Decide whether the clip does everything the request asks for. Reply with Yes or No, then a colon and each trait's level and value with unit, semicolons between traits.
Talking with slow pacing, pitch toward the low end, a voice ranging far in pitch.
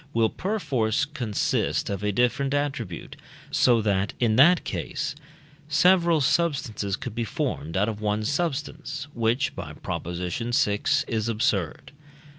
Yes: slow, 130 wpm; low, 115 Hz; wide, 5.7 semitones